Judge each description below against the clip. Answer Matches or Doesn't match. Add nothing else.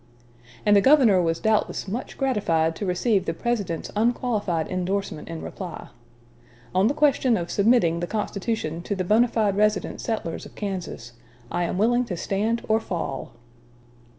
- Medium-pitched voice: Doesn't match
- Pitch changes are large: Doesn't match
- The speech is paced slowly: Doesn't match